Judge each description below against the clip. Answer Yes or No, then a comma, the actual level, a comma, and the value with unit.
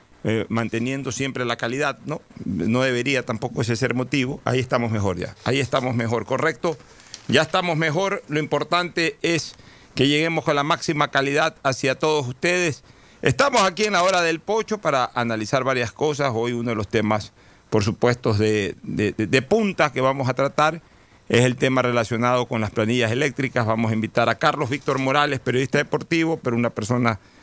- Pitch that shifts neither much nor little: Yes, average, 4.3 semitones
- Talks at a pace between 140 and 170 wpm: No, average, 180 wpm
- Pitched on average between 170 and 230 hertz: No, low, 130 Hz